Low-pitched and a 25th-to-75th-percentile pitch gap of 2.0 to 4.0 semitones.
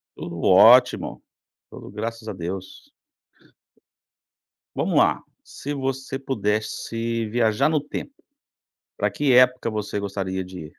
No: low, 115 Hz; average, 4.6 semitones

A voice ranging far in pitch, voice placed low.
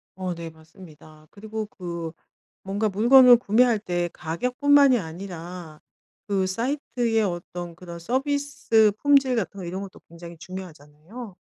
No: wide, 5.7 semitones; high, 190 Hz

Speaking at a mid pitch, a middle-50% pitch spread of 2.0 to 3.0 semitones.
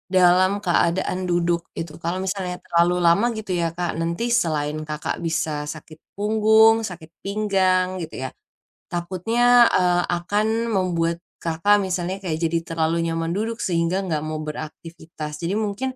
Yes: medium, 175 Hz; narrow, 2.4 semitones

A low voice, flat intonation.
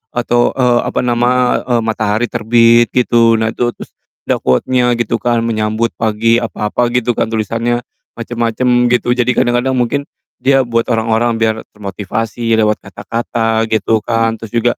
Yes: low, 115 Hz; narrow, 1.4 semitones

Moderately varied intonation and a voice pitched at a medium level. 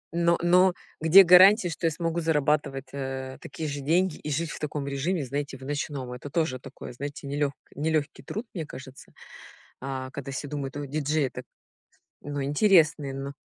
Yes: average, 3.1 semitones; medium, 145 Hz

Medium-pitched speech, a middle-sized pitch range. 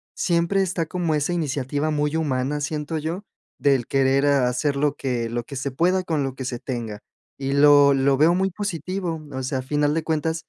Yes: medium, 145 Hz; average, 3.4 semitones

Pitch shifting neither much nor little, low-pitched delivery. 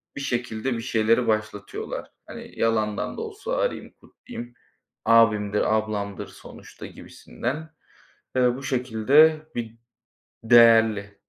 Yes: average, 3.0 semitones; low, 115 Hz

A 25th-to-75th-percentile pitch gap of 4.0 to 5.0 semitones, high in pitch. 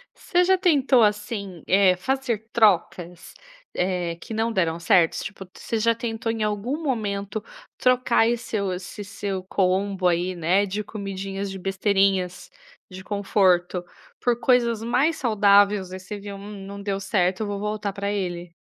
No: average, 3.0 semitones; high, 200 Hz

